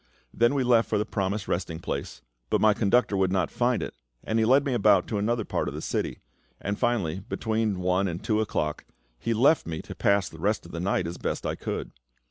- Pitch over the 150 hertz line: No, low, 105 Hz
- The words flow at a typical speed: No, fast, 230 wpm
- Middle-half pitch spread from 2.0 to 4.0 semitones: Yes, average, 3.7 semitones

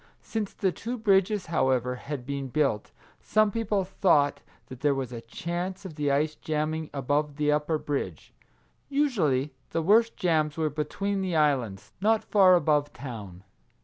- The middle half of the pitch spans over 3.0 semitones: Yes, wide, 5.4 semitones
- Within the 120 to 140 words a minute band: No, average, 155 wpm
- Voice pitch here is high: No, medium, 155 Hz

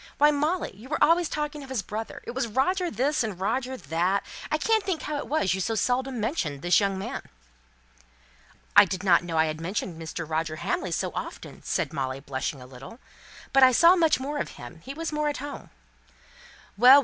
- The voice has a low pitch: No, high, 235 Hz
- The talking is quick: Yes, fast, 210 wpm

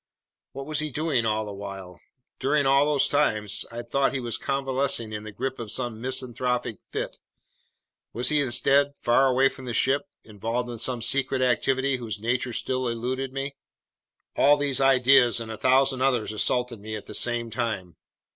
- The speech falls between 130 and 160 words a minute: No, average, 175 wpm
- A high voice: No, low, 125 Hz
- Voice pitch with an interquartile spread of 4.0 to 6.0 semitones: No, average, 2.9 semitones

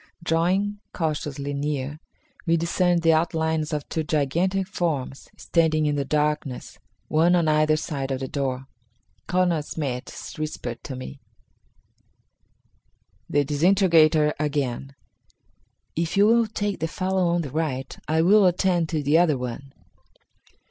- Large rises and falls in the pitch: No, average, 3.3 semitones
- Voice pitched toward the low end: No, medium, 155 Hz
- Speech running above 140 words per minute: No, slow, 135 wpm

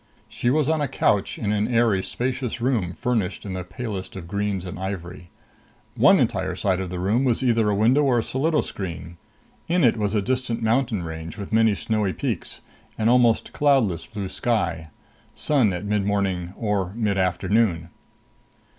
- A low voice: Yes, low, 105 Hz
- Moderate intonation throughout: Yes, average, 4.4 semitones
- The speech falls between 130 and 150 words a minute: No, average, 170 wpm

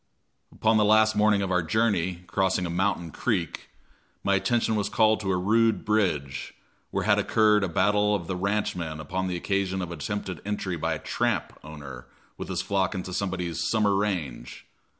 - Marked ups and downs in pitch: No, average, 3.3 semitones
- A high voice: No, very low, 95 Hz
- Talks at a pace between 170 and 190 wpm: Yes, average, 180 wpm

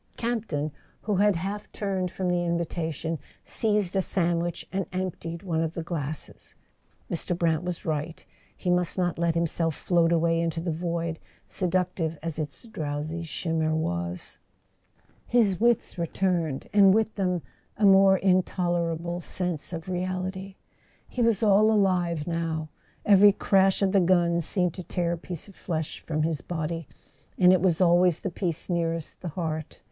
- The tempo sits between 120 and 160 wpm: Yes, average, 155 wpm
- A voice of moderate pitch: Yes, medium, 175 Hz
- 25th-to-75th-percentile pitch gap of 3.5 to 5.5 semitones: No, narrow, 2.4 semitones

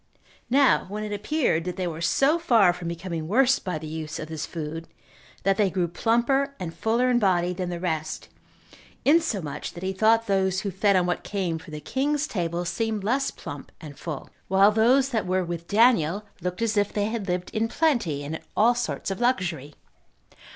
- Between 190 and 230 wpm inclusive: Yes, average, 200 wpm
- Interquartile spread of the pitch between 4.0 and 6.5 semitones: Yes, average, 5.2 semitones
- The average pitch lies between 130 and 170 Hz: No, high, 190 Hz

